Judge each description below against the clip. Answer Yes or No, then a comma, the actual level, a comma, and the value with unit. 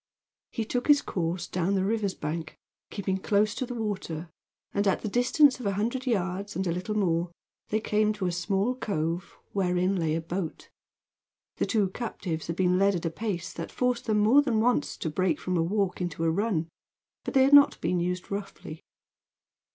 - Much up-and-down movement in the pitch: No, average, 3.8 semitones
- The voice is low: No, high, 195 Hz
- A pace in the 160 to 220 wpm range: Yes, average, 200 wpm